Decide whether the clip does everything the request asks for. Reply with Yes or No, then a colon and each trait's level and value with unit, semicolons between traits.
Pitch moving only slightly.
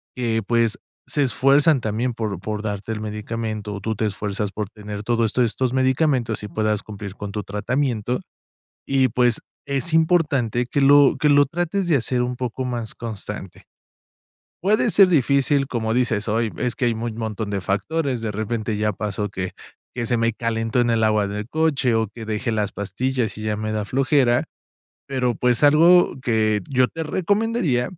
No: average, 3.8 semitones